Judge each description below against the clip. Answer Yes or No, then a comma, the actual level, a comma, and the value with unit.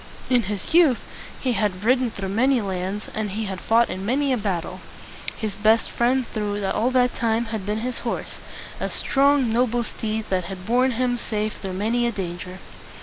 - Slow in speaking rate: No, average, 190 wpm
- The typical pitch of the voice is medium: No, high, 220 Hz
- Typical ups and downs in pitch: Yes, average, 3.6 semitones